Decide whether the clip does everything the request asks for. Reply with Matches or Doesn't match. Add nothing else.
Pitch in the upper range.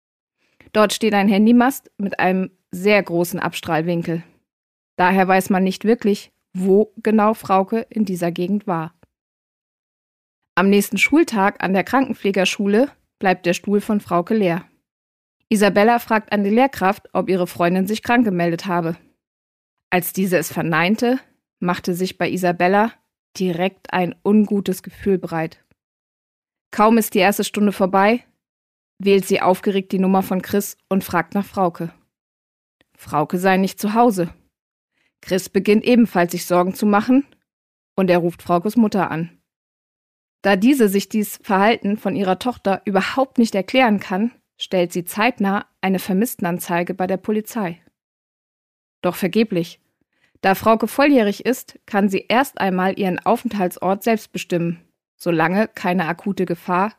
Matches